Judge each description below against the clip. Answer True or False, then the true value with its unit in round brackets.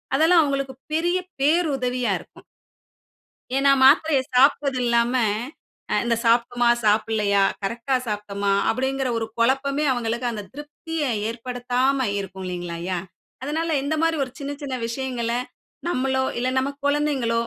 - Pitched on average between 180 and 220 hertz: False (255 Hz)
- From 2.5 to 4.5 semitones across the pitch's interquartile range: True (3.4 semitones)